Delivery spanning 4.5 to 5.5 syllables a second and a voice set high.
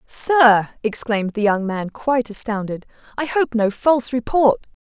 Yes: 4.7 syllables/s; high, 235 Hz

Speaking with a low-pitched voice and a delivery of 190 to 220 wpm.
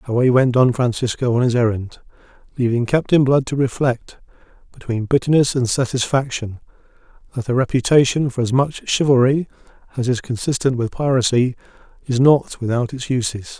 No: low, 125 Hz; average, 145 wpm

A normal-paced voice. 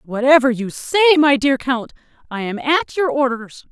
Yes: average, 180 wpm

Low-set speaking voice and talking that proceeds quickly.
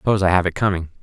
Yes: very low, 90 Hz; fast, 350 wpm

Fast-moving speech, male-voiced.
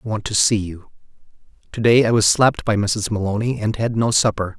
Yes: fast, 220 wpm; male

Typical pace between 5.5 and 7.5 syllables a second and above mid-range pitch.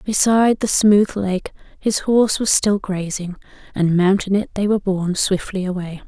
No: 5.0 syllables/s; high, 195 Hz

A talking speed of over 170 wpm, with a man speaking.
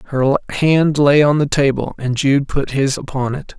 Yes: average, 200 wpm; male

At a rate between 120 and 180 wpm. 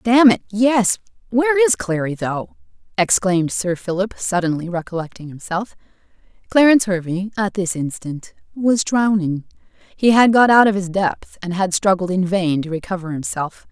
Yes: average, 145 wpm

